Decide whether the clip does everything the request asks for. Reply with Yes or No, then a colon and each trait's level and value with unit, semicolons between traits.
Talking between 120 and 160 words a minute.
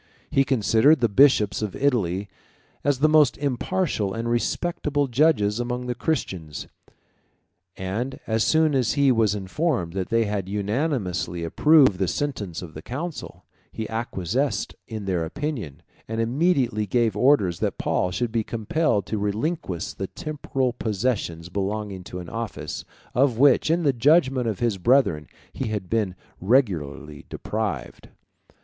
Yes: average, 145 wpm